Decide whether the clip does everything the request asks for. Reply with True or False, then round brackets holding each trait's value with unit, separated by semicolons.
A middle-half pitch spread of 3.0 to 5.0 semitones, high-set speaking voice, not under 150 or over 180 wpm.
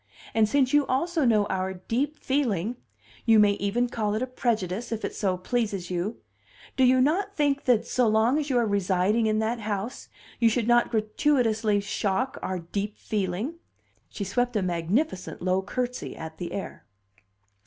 True (4.1 semitones; 220 Hz; 175 wpm)